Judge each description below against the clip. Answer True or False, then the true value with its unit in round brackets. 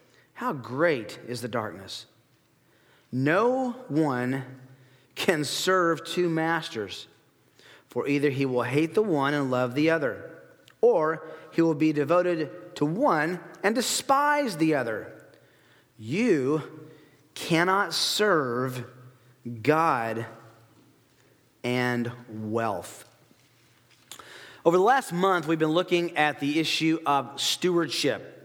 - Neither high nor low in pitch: True (155 Hz)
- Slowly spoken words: True (110 wpm)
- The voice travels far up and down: False (4.8 semitones)